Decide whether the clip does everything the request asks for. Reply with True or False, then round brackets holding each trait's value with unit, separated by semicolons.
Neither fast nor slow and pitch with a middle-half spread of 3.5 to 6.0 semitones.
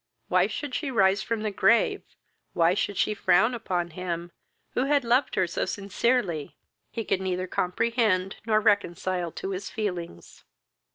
True (155 wpm; 4.3 semitones)